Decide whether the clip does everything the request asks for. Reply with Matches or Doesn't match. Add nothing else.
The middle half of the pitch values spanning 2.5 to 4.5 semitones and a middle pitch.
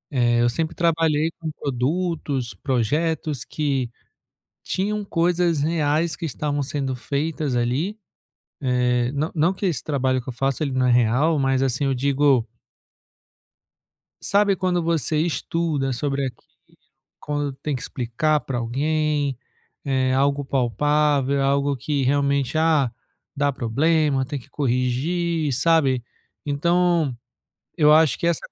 Matches